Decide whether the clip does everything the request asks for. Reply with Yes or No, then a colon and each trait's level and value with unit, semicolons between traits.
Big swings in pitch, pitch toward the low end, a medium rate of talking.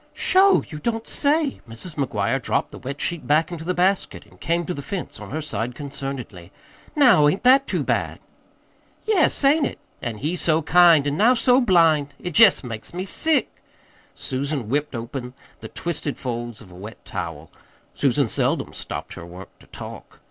No: wide, 7.2 semitones; medium, 150 Hz; average, 180 wpm